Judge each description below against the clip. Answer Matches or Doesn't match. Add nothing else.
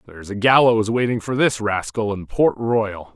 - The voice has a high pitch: Doesn't match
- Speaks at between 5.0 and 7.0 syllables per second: Doesn't match